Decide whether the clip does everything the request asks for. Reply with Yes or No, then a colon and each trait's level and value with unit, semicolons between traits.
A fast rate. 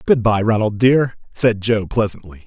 No: average, 170 wpm